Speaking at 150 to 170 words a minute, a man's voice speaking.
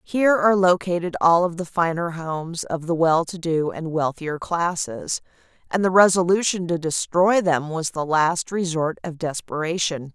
No: average, 165 wpm; female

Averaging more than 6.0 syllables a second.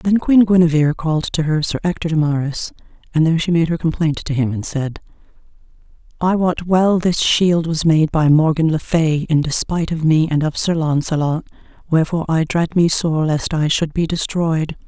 No: 5.1 syllables/s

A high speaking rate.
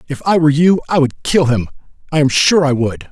Yes: fast, 230 wpm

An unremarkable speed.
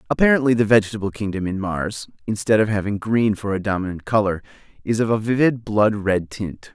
Yes: average, 185 wpm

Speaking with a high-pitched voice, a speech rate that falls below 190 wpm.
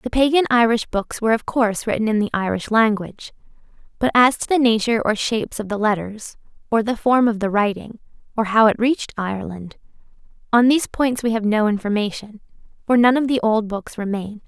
No: high, 225 Hz; average, 195 wpm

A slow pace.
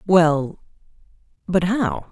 Yes: slow, 85 wpm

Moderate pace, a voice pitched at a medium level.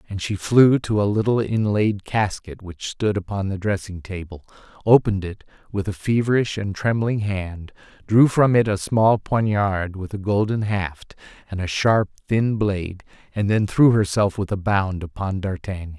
No: average, 175 wpm; low, 100 Hz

